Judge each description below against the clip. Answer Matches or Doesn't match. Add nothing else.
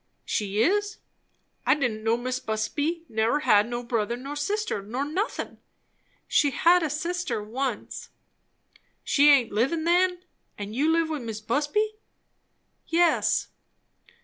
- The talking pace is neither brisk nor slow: Doesn't match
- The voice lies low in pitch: Doesn't match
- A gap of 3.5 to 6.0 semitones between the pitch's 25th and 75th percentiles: Doesn't match